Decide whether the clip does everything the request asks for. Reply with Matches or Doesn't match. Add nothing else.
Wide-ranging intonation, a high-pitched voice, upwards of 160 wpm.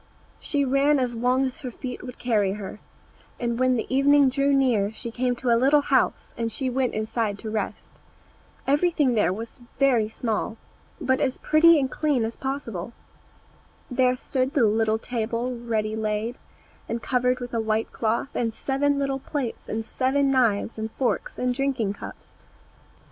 Doesn't match